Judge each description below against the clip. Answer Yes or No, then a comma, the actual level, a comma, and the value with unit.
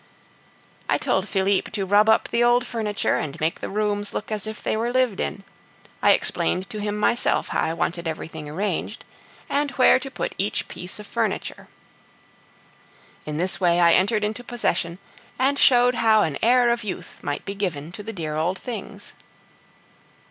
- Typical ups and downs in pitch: Yes, average, 4.7 semitones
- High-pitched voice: Yes, high, 205 Hz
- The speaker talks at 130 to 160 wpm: No, average, 175 wpm